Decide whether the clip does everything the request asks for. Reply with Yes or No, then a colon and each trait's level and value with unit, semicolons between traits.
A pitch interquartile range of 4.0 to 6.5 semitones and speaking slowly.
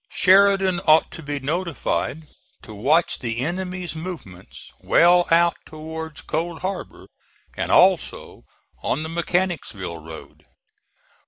Yes: average, 4.5 semitones; slow, 110 wpm